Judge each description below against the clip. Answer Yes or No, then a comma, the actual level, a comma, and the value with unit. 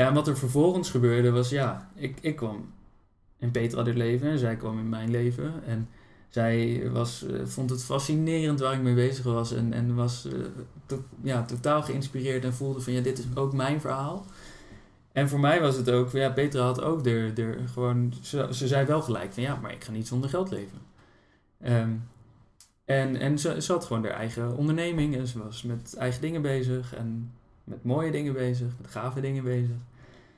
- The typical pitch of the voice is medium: No, low, 125 Hz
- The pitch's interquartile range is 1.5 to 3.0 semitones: Yes, narrow, 2.5 semitones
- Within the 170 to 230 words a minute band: Yes, fast, 200 wpm